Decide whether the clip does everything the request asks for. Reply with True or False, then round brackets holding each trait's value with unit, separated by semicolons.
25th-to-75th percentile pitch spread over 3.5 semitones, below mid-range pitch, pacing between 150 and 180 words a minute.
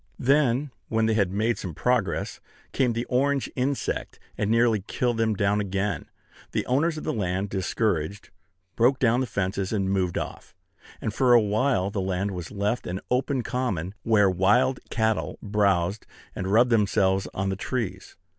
True (4.2 semitones; 105 Hz; 165 wpm)